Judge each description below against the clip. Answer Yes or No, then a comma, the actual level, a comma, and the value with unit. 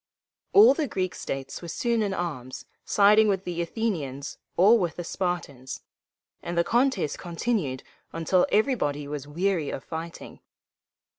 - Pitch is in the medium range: Yes, medium, 175 Hz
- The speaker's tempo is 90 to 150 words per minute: Yes, average, 140 wpm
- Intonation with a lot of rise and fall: Yes, wide, 6.1 semitones